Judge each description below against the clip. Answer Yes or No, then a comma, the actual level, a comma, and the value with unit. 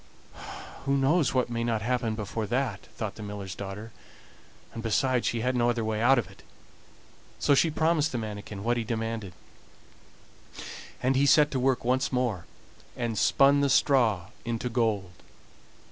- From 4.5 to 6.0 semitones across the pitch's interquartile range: No, average, 3.3 semitones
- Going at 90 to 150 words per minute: No, average, 160 wpm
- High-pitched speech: No, low, 120 Hz